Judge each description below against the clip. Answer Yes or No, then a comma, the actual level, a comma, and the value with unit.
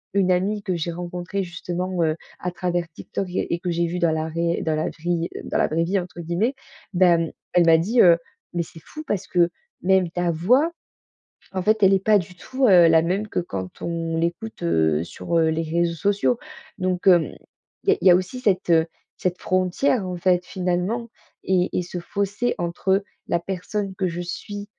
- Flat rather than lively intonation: Yes, narrow, 2.2 semitones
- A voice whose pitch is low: No, medium, 180 Hz